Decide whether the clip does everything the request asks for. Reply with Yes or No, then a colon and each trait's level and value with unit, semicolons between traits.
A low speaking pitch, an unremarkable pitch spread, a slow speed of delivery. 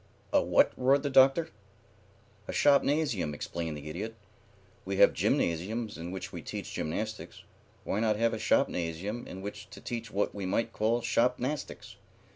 No: low, 110 Hz; average, 4.8 semitones; average, 155 wpm